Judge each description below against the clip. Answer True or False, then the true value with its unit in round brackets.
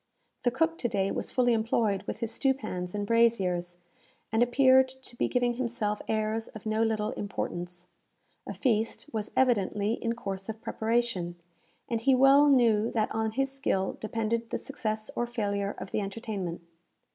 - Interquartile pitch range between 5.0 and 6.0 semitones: False (2.8 semitones)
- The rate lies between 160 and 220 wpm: True (165 wpm)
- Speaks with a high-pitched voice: True (225 Hz)